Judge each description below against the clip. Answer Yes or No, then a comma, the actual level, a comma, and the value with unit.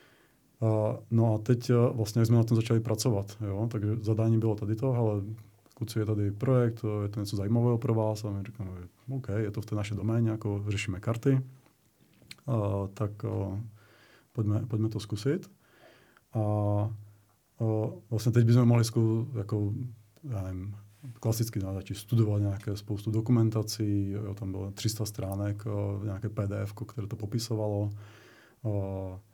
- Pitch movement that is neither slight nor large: No, narrow, 1.9 semitones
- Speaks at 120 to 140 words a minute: No, average, 165 wpm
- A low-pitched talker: Yes, low, 110 Hz